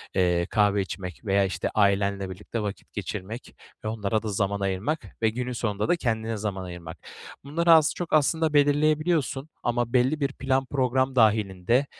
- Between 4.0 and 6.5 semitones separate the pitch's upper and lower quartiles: Yes, wide, 5.4 semitones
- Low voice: Yes, low, 110 Hz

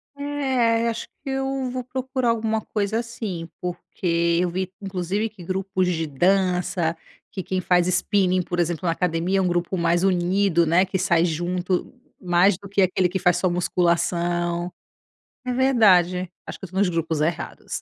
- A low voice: No, medium, 185 Hz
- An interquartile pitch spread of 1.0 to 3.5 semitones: Yes, average, 2.9 semitones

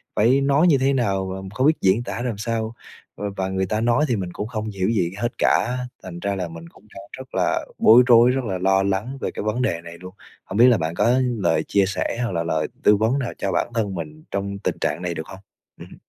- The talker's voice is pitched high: No, low, 105 Hz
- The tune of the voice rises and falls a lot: No, average, 4.2 semitones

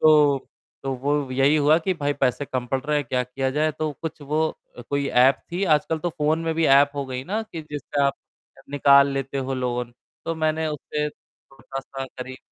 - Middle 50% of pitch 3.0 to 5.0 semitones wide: No, narrow, 2.5 semitones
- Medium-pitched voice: Yes, medium, 145 Hz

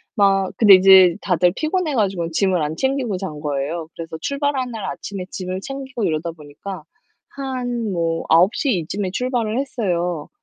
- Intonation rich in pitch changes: Yes, wide, 6.5 semitones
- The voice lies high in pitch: Yes, high, 195 Hz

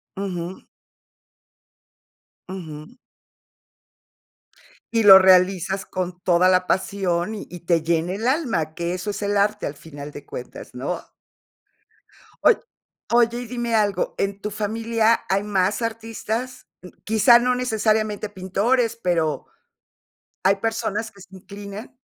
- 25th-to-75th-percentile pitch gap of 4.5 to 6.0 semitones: No, average, 3.7 semitones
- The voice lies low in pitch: No, high, 200 Hz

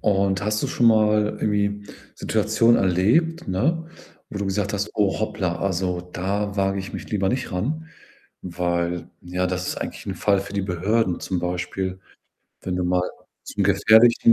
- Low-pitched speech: Yes, low, 100 Hz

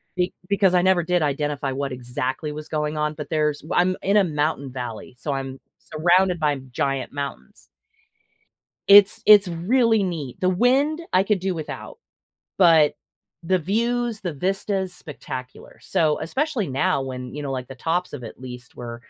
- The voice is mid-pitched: Yes, medium, 160 Hz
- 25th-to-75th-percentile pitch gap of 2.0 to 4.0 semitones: No, wide, 5.6 semitones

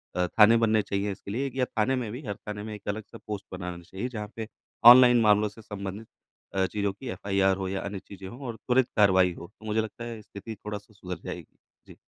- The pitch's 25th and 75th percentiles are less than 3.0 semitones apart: Yes, narrow, 2.5 semitones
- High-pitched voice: No, low, 105 Hz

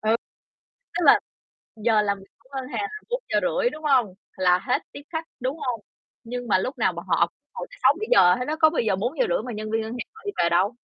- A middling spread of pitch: No, wide, 7.2 semitones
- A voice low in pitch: No, high, 245 Hz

